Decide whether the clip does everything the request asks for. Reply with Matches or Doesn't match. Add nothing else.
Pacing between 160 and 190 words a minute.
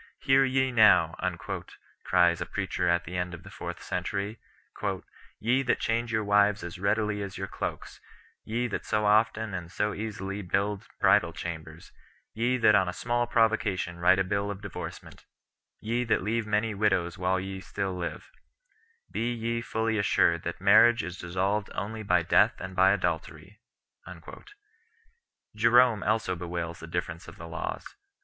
Matches